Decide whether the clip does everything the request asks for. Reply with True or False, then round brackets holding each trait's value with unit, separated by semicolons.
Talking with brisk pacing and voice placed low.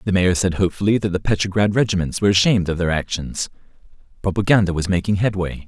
False (180 wpm; 95 Hz)